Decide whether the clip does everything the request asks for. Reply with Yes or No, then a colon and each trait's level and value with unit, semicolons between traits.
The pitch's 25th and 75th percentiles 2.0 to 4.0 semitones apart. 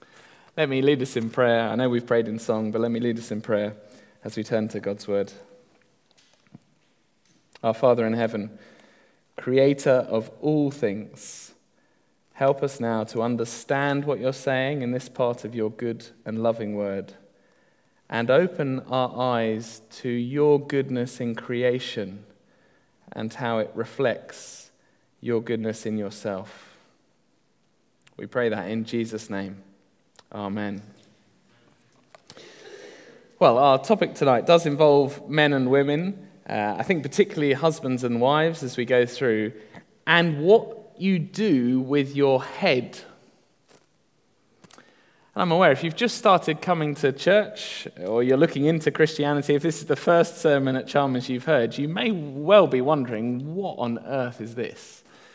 No: average, 4.7 semitones